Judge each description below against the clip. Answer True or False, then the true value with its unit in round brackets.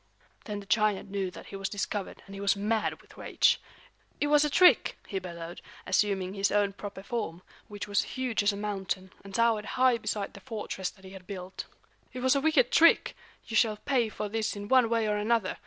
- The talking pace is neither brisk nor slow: False (215 wpm)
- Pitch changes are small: False (3.0 semitones)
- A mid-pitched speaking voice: False (205 Hz)